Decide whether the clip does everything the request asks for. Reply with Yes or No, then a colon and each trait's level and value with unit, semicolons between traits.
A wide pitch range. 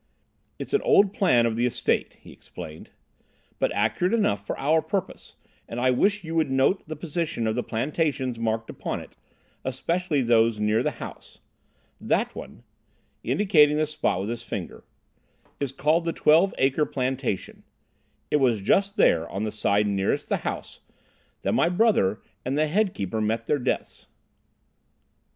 Yes: wide, 6.4 semitones